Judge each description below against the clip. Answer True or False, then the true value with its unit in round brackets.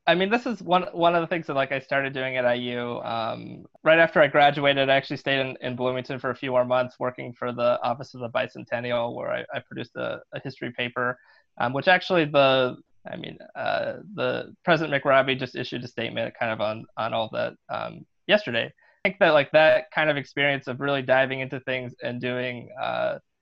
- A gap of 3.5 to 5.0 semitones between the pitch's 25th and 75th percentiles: True (3.8 semitones)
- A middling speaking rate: False (220 wpm)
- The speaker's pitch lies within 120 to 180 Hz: True (135 Hz)